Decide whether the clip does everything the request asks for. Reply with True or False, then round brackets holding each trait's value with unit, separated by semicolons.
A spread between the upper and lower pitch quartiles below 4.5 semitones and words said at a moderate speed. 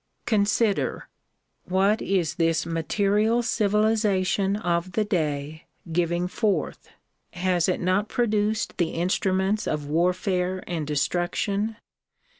False (3.5 semitones; 100 wpm)